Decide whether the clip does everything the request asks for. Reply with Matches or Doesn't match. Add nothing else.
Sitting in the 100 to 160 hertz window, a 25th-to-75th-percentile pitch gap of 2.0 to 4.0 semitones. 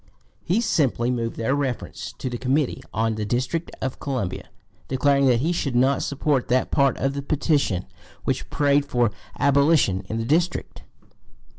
Matches